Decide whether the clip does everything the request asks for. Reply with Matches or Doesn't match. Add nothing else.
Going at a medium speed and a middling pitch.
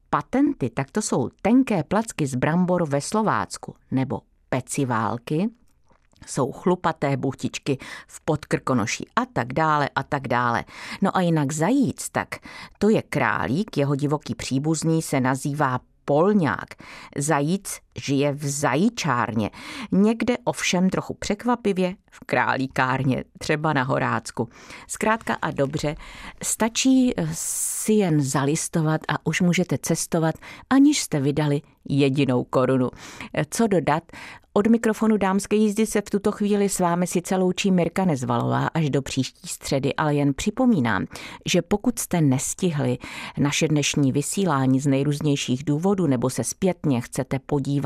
Matches